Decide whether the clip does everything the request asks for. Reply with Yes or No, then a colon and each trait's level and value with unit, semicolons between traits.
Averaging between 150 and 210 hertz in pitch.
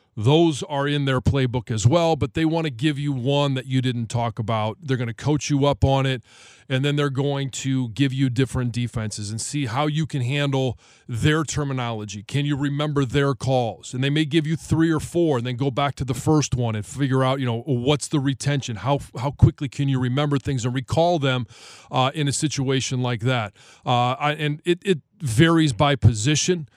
No: low, 135 Hz